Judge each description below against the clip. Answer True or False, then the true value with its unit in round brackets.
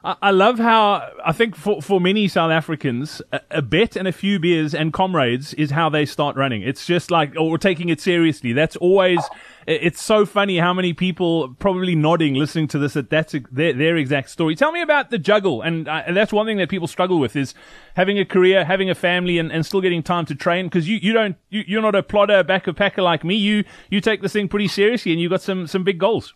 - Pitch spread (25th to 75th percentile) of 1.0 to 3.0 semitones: False (3.7 semitones)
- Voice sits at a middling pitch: True (180 Hz)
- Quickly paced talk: True (245 wpm)